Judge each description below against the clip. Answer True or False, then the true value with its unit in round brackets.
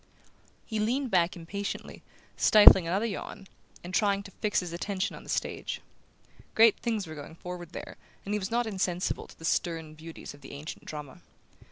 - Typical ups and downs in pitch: True (4.1 semitones)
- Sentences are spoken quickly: False (180 wpm)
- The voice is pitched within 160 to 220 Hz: True (185 Hz)